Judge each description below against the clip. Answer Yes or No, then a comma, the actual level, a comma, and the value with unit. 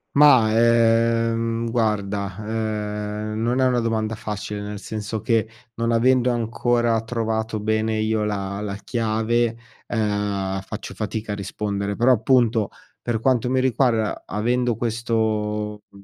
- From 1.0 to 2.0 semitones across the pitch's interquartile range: Yes, narrow, 1.7 semitones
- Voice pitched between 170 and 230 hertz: No, low, 110 Hz